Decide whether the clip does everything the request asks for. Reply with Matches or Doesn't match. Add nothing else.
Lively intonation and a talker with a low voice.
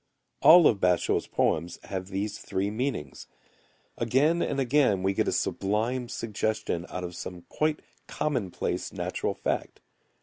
Matches